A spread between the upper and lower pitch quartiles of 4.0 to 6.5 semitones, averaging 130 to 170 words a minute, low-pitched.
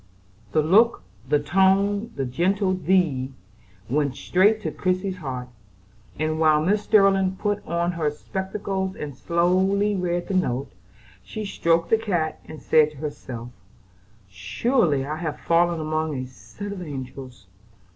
No: average, 4.6 semitones; average, 140 wpm; medium, 170 Hz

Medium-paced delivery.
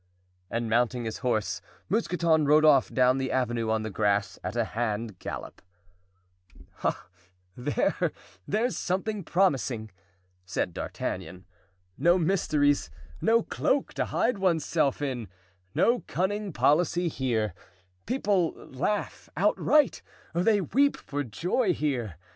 No: slow, 120 wpm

